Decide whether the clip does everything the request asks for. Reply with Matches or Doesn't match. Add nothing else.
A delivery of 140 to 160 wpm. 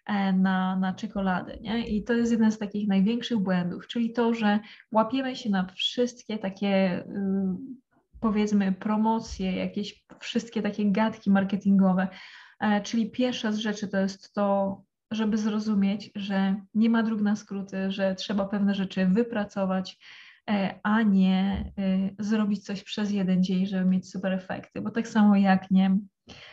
Matches